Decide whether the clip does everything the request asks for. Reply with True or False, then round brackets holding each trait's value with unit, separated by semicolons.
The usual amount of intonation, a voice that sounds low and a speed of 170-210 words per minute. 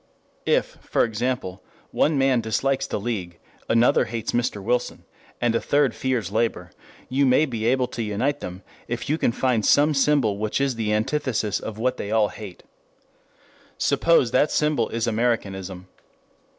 False (3.7 semitones; 115 Hz; 160 wpm)